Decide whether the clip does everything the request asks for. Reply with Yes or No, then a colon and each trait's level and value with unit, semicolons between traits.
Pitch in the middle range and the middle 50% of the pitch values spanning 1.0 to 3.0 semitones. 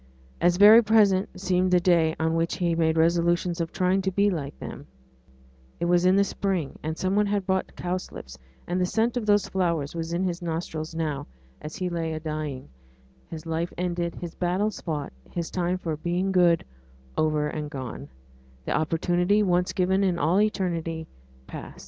Yes: medium, 175 Hz; narrow, 2.5 semitones